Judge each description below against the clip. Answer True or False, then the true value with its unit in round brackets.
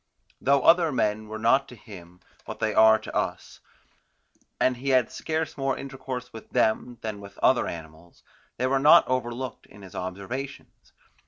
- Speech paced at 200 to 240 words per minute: False (165 wpm)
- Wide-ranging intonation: False (4.1 semitones)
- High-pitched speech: False (120 Hz)